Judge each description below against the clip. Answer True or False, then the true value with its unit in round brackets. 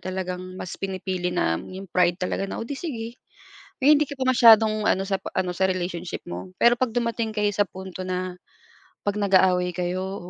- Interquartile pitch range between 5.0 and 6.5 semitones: False (3.2 semitones)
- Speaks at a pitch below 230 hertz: True (190 Hz)